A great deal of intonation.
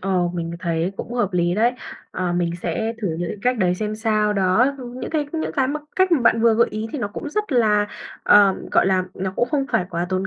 No: average, 5.0 semitones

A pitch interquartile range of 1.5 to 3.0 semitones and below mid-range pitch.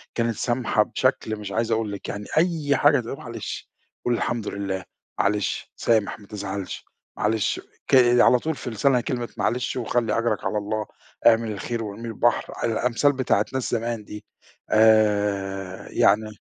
Yes: narrow, 2.5 semitones; low, 110 Hz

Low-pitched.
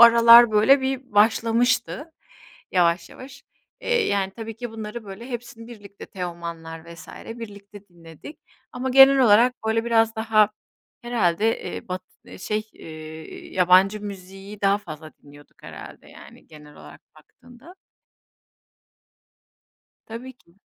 No: high, 215 Hz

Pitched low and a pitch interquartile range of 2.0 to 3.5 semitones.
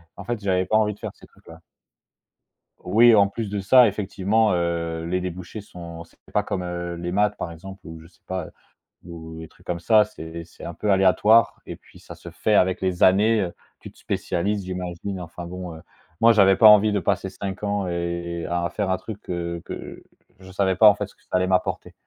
Yes: very low, 95 Hz; average, 3.0 semitones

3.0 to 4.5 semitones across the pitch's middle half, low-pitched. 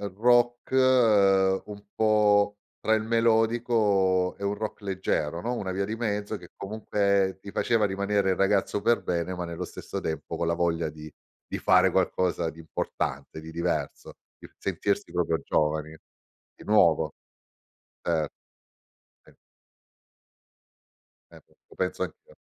Yes: average, 4.0 semitones; low, 100 Hz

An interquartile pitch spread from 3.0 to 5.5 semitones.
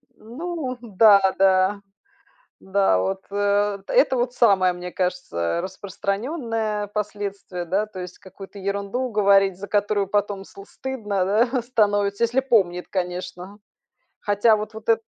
No: narrow, 2.5 semitones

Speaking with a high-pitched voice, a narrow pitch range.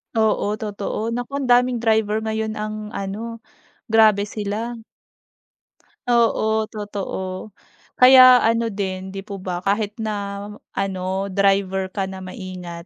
Yes: high, 210 Hz; narrow, 2.3 semitones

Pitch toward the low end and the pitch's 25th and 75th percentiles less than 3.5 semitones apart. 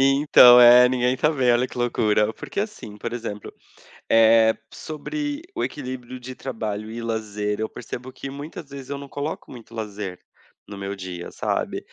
No: low, 120 Hz; average, 3.9 semitones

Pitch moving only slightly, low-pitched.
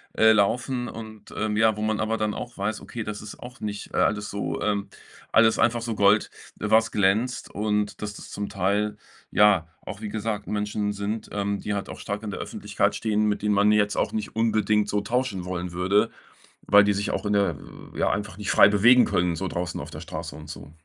Yes: narrow, 1.3 semitones; low, 105 Hz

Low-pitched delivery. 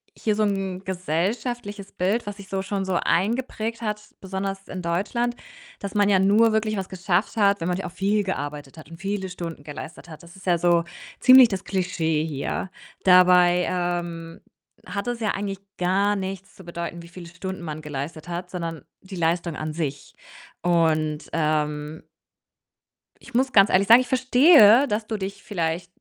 No: medium, 185 Hz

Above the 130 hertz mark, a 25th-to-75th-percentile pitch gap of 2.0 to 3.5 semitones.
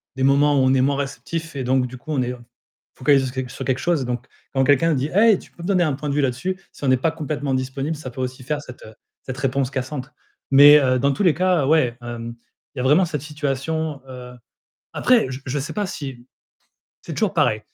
Yes: medium, 140 Hz; average, 2.9 semitones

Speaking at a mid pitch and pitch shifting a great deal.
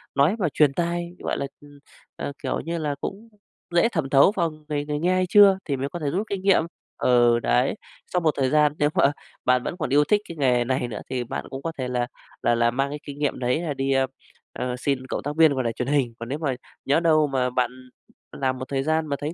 No: medium, 145 Hz; average, 3.7 semitones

